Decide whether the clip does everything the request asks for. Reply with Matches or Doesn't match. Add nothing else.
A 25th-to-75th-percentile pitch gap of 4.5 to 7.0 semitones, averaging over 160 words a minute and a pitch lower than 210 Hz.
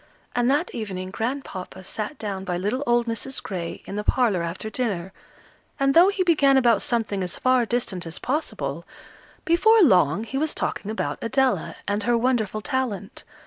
Doesn't match